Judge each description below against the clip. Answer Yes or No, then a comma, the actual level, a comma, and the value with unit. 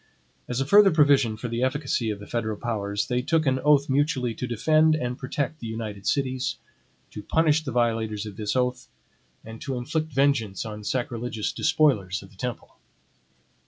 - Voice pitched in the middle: No, low, 125 Hz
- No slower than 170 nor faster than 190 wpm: Yes, average, 175 wpm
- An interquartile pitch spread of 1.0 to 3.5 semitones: No, average, 4.1 semitones